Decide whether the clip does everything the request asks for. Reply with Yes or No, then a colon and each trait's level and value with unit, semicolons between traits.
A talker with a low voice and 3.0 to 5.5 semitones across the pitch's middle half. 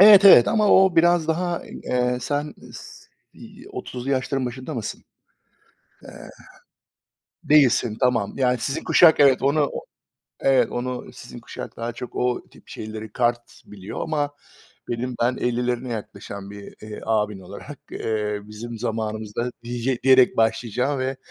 Yes: low, 125 Hz; average, 3.5 semitones